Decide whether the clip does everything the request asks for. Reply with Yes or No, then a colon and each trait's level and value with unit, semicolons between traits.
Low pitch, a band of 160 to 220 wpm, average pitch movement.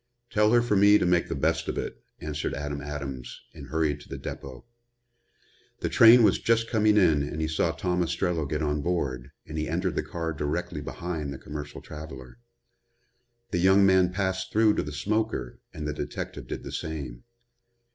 Yes: very low, 80 Hz; average, 185 wpm; average, 4.4 semitones